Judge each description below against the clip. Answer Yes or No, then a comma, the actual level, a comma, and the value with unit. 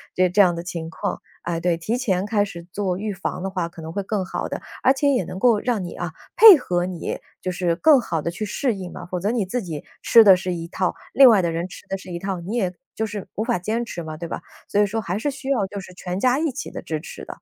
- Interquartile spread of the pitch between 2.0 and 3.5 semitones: No, average, 4.0 semitones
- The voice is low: No, high, 190 Hz